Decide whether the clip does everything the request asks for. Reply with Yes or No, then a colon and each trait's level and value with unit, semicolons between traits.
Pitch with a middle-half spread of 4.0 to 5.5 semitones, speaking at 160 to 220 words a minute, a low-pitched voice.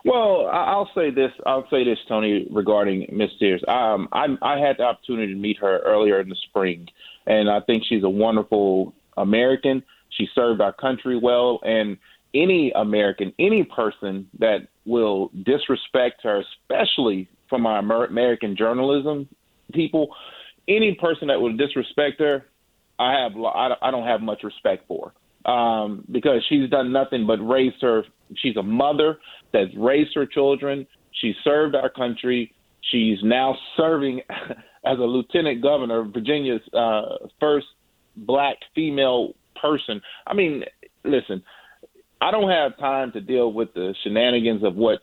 No: average, 4.6 semitones; average, 150 wpm; low, 125 Hz